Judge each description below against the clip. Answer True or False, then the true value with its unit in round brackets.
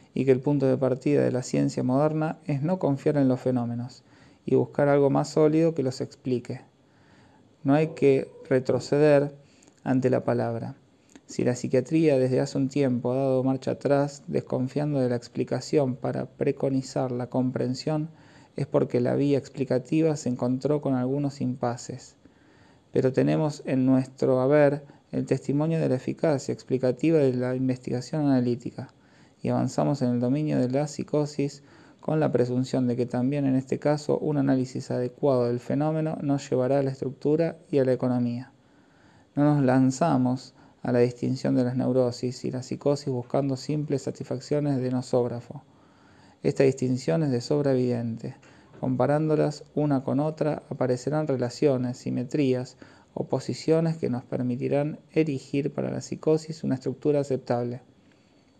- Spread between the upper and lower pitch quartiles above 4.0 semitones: False (2.6 semitones)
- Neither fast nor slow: True (150 wpm)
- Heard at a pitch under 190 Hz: True (135 Hz)